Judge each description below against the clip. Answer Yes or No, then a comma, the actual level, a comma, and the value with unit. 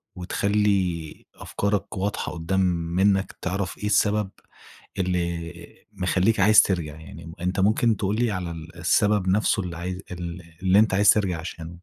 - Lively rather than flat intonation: No, average, 2.9 semitones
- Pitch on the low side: Yes, very low, 95 Hz